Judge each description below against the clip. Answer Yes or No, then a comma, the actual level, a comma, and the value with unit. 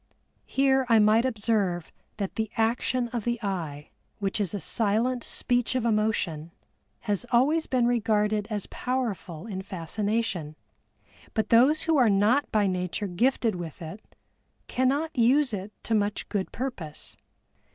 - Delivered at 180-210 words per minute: No, average, 140 wpm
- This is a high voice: Yes, high, 220 Hz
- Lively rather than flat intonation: No, average, 4.0 semitones